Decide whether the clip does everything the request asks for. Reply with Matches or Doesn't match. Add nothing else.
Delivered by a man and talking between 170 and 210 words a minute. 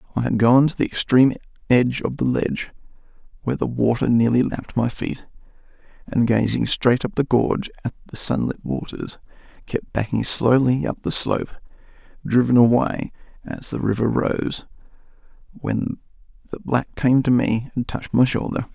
Doesn't match